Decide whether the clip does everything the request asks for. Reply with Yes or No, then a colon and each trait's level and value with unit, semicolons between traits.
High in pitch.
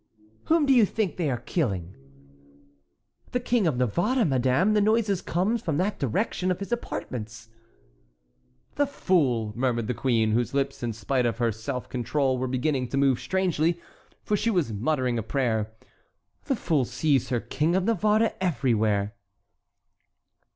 No: medium, 140 Hz